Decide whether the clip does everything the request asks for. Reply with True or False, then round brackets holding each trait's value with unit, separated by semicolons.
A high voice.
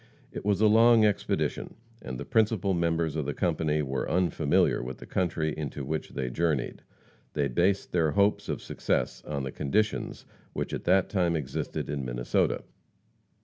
False (80 Hz)